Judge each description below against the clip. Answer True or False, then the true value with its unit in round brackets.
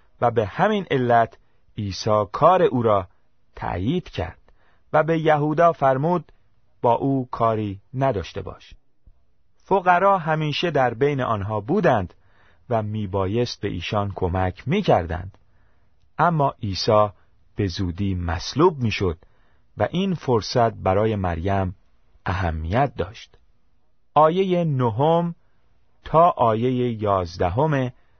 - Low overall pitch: True (110 Hz)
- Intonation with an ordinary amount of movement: False (6.3 semitones)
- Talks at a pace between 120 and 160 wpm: False (105 wpm)